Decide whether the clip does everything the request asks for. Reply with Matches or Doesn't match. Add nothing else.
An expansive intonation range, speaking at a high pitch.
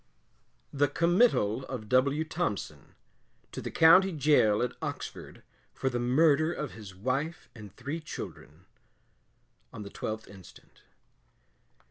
Doesn't match